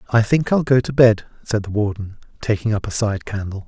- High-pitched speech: No, low, 110 Hz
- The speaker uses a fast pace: Yes, fast, 230 wpm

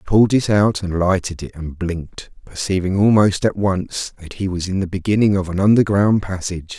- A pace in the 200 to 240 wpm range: Yes, fast, 205 wpm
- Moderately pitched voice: No, very low, 95 Hz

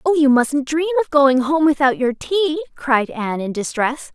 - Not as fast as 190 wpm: No, fast, 205 wpm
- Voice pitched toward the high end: Yes, very high, 280 Hz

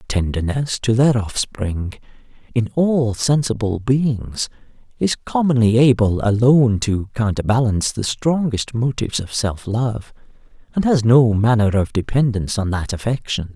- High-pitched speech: No, low, 115 Hz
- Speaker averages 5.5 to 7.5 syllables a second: No, 4.5 syllables/s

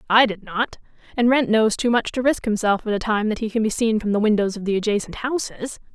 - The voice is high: Yes, high, 220 Hz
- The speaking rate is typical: No, fast, 260 wpm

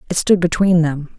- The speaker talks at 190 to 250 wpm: Yes, fast, 205 wpm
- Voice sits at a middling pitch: Yes, medium, 170 Hz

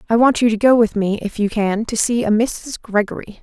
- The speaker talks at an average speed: No, fast, 265 wpm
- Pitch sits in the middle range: No, high, 220 Hz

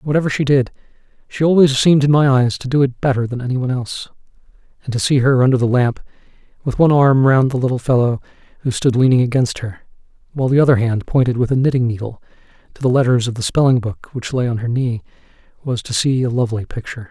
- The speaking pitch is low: Yes, low, 125 Hz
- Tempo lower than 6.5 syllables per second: No, 6.6 syllables/s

